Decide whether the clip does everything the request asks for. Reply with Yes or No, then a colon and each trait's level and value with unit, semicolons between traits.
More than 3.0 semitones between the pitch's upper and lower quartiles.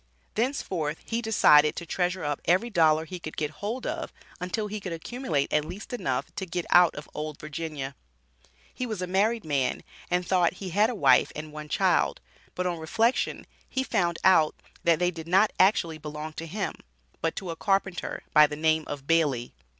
Yes: average, 4.2 semitones